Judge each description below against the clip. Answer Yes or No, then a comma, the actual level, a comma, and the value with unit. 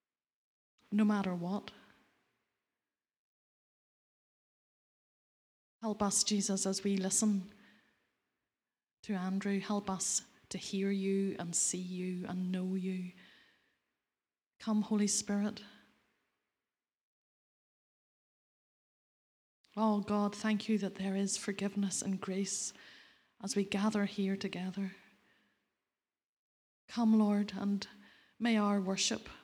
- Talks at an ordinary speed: No, slow, 95 wpm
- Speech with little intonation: Yes, narrow, 1.3 semitones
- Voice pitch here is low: No, high, 200 Hz